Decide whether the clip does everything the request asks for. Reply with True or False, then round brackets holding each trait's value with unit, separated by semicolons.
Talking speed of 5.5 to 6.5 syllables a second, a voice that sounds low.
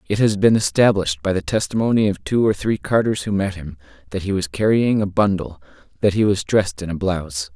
True (5.9 syllables/s; 100 Hz)